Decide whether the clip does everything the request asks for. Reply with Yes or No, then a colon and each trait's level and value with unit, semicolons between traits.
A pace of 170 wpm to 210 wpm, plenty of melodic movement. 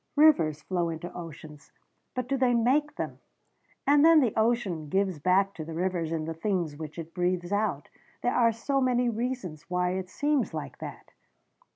Yes: average, 180 wpm; wide, 6.8 semitones